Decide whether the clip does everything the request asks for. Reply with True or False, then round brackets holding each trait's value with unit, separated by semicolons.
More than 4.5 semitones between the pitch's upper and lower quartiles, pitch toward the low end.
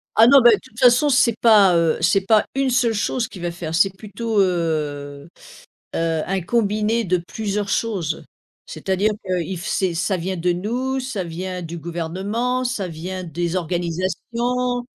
False (5.0 semitones; 190 Hz)